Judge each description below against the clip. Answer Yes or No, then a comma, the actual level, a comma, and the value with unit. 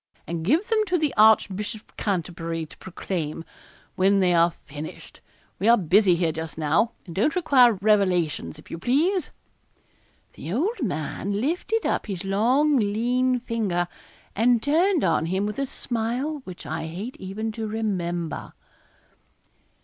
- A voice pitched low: No, high, 205 Hz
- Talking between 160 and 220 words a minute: No, average, 150 wpm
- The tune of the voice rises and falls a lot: Yes, wide, 6.3 semitones